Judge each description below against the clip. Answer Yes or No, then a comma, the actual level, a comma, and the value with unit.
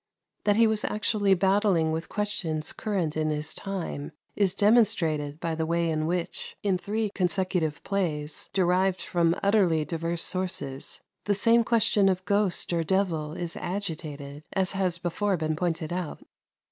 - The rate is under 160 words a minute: Yes, average, 150 wpm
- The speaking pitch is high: No, medium, 180 Hz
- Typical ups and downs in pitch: Yes, average, 3.9 semitones